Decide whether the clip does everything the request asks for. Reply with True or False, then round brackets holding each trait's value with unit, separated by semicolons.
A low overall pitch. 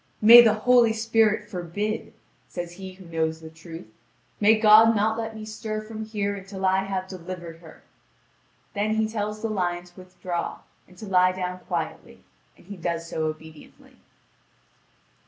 False (195 Hz)